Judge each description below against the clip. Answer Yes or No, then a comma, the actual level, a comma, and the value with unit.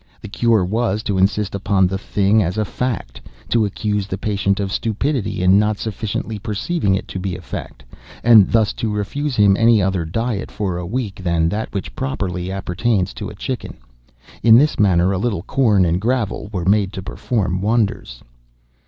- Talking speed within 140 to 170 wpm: No, average, 180 wpm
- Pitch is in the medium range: No, low, 100 Hz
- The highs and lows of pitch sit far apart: No, average, 2.9 semitones